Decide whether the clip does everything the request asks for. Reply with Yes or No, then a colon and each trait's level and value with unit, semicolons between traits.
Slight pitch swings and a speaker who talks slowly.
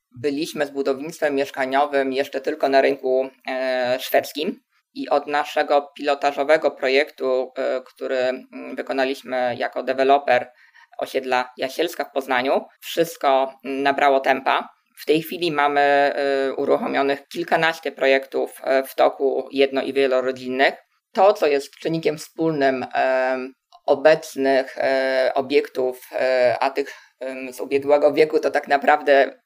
Yes: narrow, 1.8 semitones; slow, 105 wpm